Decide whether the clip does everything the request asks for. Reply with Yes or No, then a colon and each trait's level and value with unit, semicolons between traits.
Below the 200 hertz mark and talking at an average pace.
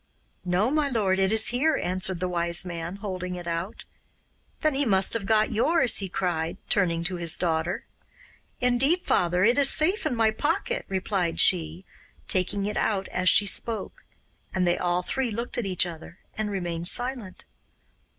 Yes: high, 190 Hz; average, 170 wpm